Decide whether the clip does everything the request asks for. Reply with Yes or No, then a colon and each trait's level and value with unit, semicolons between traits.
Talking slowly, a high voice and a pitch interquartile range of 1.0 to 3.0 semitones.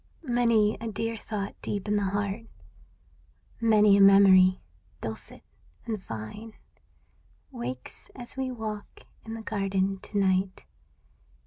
Yes: slow, 125 wpm; high, 205 Hz; narrow, 2.6 semitones